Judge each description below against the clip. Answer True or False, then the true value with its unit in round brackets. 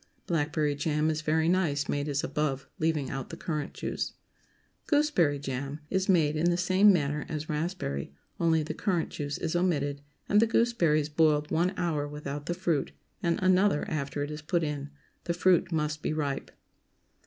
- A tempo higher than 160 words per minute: True (175 wpm)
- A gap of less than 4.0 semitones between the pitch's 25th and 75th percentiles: True (3.0 semitones)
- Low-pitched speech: False (155 Hz)